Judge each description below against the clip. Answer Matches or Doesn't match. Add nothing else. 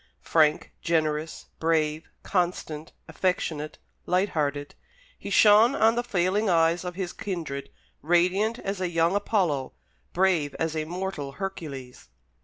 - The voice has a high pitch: Doesn't match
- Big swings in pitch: Doesn't match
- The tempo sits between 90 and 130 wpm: Matches